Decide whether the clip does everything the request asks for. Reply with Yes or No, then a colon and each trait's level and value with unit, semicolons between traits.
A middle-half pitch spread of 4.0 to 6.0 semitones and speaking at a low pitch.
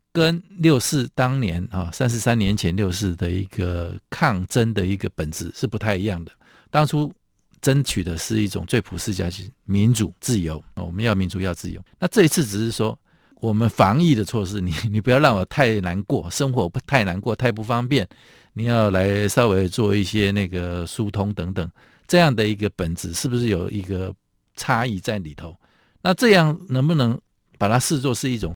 Yes: average, 5.1 semitones; low, 110 Hz